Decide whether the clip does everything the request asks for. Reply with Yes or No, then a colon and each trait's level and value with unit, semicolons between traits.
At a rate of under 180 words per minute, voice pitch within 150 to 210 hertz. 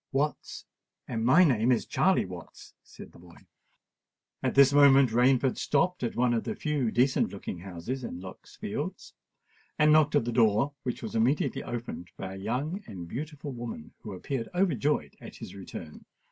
No: average, 170 wpm; low, 125 Hz